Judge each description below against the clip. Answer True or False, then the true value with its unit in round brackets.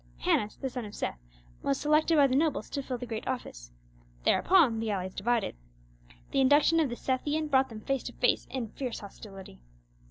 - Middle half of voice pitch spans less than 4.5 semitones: False (4.9 semitones)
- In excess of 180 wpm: True (190 wpm)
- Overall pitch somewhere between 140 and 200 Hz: False (255 Hz)